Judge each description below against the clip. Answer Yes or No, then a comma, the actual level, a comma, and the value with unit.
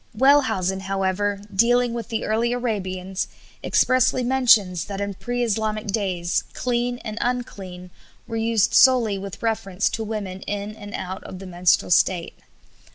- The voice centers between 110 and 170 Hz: No, high, 210 Hz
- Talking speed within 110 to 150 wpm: Yes, average, 145 wpm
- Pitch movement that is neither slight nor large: Yes, average, 3.7 semitones